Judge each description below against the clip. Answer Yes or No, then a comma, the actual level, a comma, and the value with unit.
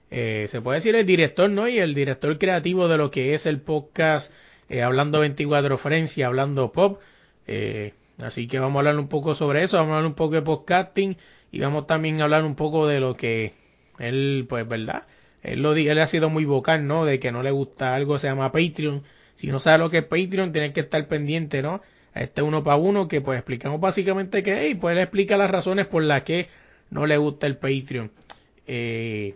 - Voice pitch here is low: No, medium, 150 Hz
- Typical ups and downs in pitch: Yes, average, 3.1 semitones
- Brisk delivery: Yes, fast, 220 wpm